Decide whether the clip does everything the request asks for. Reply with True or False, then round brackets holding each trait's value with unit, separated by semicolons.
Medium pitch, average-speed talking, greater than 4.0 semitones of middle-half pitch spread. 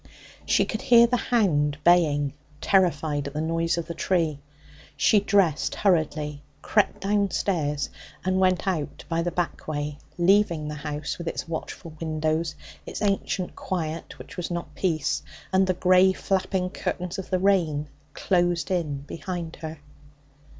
False (170 Hz; 150 wpm; 3.4 semitones)